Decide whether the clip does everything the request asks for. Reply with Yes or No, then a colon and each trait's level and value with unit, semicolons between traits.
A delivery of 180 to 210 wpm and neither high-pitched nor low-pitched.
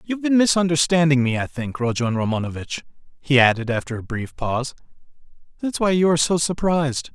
No: average, 170 wpm; medium, 145 Hz